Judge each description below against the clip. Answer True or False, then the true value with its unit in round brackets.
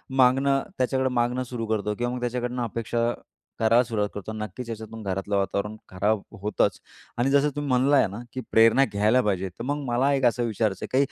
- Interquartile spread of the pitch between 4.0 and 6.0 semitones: False (3.3 semitones)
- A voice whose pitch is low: True (120 Hz)